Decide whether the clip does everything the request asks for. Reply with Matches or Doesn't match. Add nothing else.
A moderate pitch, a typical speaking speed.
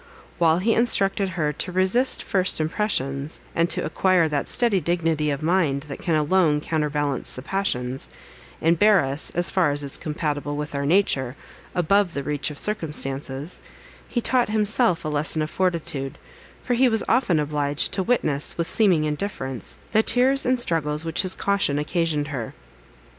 Matches